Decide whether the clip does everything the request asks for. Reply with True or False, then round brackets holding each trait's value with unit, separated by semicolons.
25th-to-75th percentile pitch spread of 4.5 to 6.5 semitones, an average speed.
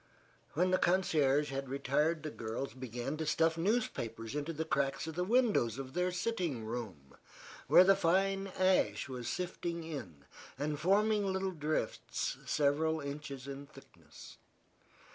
True (5.0 semitones; 145 wpm)